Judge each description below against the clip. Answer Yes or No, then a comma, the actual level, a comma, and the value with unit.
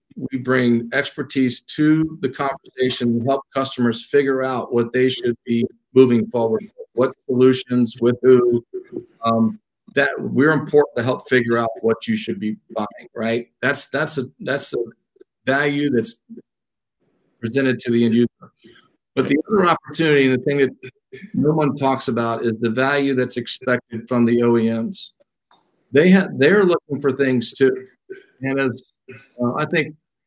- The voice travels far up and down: No, average, 3.5 semitones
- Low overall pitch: Yes, low, 130 Hz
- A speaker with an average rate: Yes, average, 160 wpm